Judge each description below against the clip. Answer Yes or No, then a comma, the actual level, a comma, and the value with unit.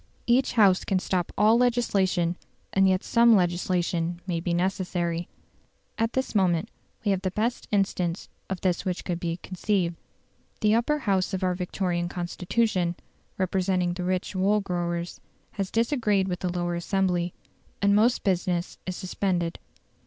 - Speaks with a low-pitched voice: No, medium, 185 Hz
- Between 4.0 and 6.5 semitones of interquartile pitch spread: No, narrow, 2.5 semitones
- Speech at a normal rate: Yes, average, 150 wpm